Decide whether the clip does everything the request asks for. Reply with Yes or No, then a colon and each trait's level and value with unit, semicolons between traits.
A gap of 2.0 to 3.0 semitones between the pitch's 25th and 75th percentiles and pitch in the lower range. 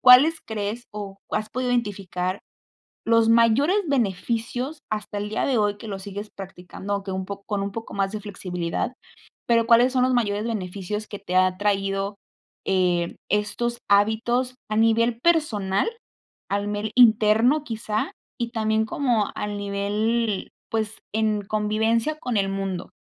No: average, 2.7 semitones; high, 215 Hz